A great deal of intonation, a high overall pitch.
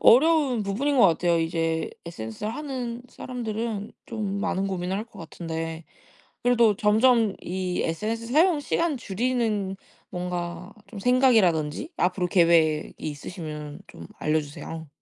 Yes: wide, 6.1 semitones; high, 195 Hz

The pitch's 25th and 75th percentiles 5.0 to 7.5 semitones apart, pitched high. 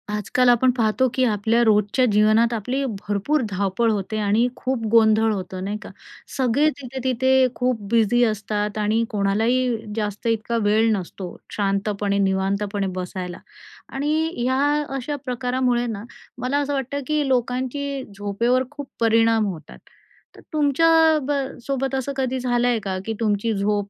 No: average, 3.7 semitones; high, 230 Hz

